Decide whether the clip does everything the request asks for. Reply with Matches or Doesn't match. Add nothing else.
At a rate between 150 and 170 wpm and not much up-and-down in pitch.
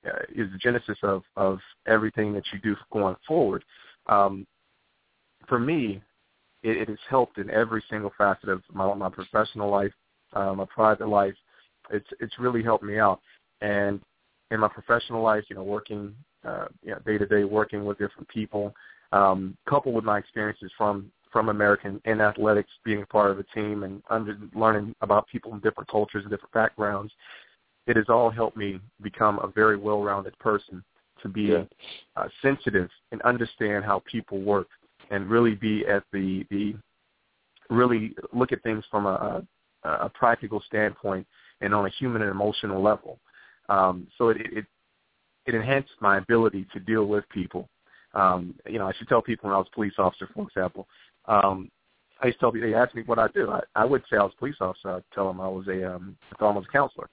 Doesn't match